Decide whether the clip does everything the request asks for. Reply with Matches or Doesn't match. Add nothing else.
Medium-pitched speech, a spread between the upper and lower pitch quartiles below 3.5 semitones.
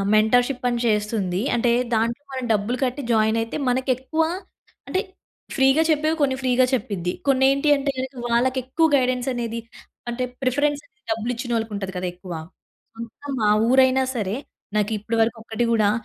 Doesn't match